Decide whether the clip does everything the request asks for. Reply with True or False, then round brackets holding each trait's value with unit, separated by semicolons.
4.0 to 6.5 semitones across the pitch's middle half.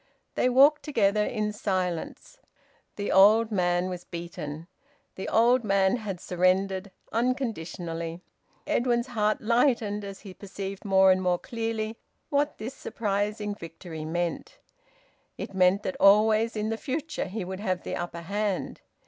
False (3.6 semitones)